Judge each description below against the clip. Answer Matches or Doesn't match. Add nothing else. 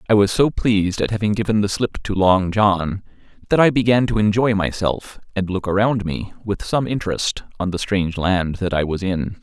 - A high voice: Doesn't match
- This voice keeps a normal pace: Doesn't match